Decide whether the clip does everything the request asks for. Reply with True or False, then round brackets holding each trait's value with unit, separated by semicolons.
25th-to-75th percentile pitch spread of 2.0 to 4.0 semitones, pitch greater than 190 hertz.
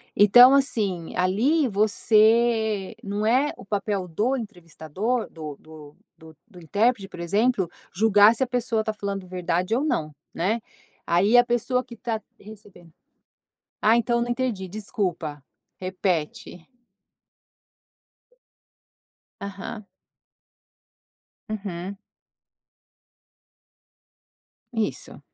False (4.4 semitones; 205 Hz)